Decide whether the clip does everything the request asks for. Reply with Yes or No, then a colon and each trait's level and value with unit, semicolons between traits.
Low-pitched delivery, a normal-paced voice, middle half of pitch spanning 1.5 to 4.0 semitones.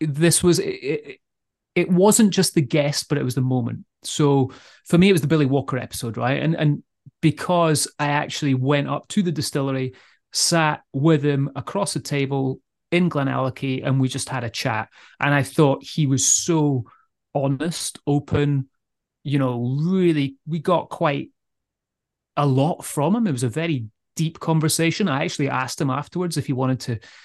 No: medium, 145 Hz; average, 180 wpm; average, 3.5 semitones